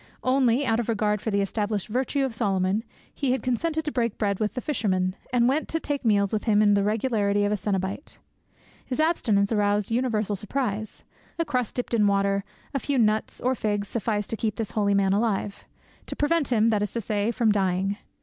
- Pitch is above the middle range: Yes, high, 215 Hz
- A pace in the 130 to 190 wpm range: No, fast, 205 wpm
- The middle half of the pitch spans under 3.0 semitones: No, average, 3.5 semitones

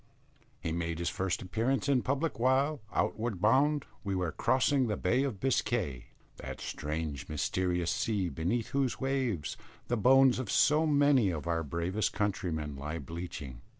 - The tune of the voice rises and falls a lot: Yes, wide, 7.8 semitones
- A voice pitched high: No, low, 105 Hz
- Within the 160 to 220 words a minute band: No, average, 150 wpm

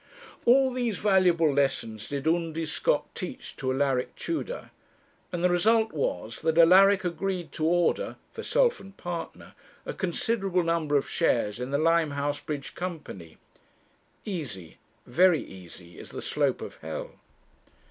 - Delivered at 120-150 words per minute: Yes, average, 140 wpm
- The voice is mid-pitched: Yes, medium, 165 Hz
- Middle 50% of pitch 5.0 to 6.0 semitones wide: Yes, average, 5.3 semitones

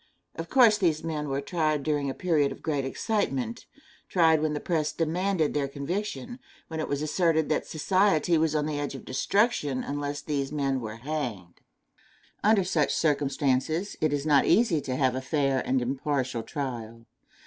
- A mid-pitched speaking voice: Yes, medium, 150 Hz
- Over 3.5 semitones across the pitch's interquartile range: No, average, 3.2 semitones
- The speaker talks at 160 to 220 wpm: Yes, average, 170 wpm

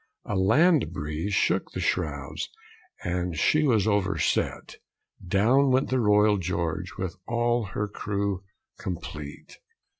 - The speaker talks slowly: Yes, slow, 120 wpm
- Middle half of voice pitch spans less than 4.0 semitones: No, average, 4.4 semitones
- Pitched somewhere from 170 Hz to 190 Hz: No, low, 100 Hz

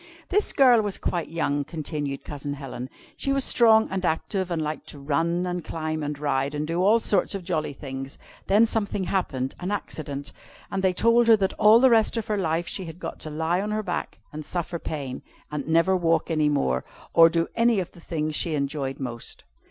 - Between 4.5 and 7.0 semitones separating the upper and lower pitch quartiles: Yes, average, 4.8 semitones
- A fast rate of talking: Yes, fast, 215 wpm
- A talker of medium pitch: Yes, medium, 165 Hz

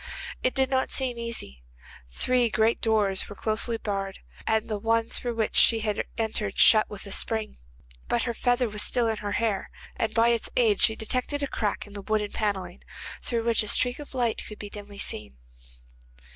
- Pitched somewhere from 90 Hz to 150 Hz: No, high, 220 Hz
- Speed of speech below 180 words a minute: No, average, 200 wpm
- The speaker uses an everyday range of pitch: No, narrow, 2.3 semitones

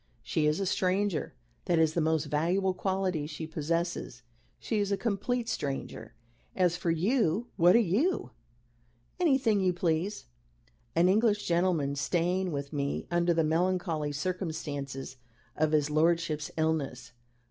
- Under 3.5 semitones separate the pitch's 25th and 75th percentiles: No, average, 3.8 semitones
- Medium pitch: Yes, medium, 170 Hz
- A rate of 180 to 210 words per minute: No, slow, 135 wpm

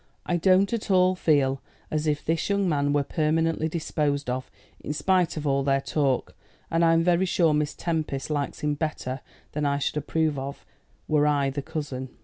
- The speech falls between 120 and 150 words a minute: No, average, 185 wpm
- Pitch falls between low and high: Yes, medium, 150 Hz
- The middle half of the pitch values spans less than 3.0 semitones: Yes, narrow, 2.6 semitones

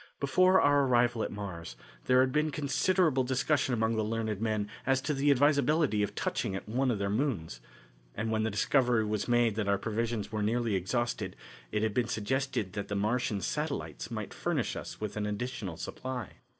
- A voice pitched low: Yes, low, 115 Hz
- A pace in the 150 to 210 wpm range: Yes, average, 190 wpm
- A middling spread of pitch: Yes, average, 4.1 semitones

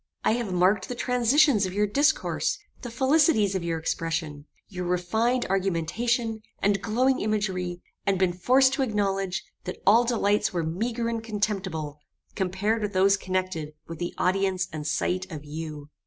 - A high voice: Yes, high, 195 Hz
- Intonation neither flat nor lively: Yes, average, 4.3 semitones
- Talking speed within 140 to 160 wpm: Yes, average, 155 wpm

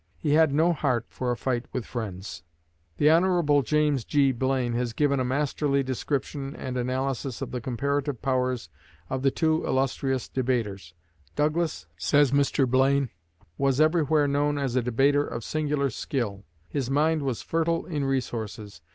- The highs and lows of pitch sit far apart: No, average, 2.9 semitones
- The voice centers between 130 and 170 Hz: Yes, low, 135 Hz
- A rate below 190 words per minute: Yes, average, 155 wpm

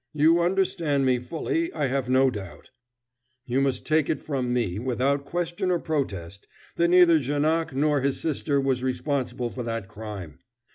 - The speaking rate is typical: Yes, average, 160 wpm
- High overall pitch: No, medium, 140 Hz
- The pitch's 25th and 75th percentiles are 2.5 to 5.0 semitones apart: Yes, average, 4.3 semitones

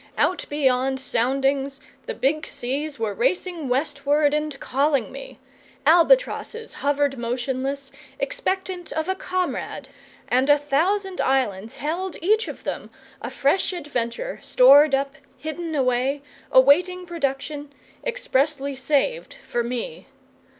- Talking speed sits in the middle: No, slow, 115 wpm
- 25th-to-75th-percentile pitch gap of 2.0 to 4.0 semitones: No, average, 4.8 semitones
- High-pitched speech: Yes, very high, 285 Hz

